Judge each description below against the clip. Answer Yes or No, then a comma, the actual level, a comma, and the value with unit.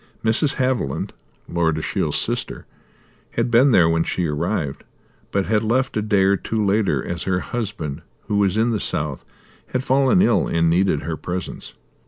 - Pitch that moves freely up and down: Yes, wide, 5.8 semitones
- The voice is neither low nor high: No, low, 100 Hz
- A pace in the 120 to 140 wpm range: No, average, 170 wpm